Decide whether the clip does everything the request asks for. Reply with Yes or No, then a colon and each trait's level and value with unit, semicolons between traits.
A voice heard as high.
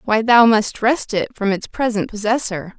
Yes: high, 220 Hz